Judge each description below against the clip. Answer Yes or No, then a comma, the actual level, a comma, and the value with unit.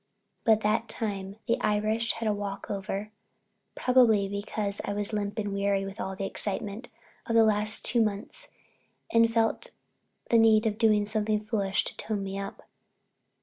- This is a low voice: No, high, 210 Hz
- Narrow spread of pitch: Yes, narrow, 1.9 semitones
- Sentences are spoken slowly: No, average, 165 wpm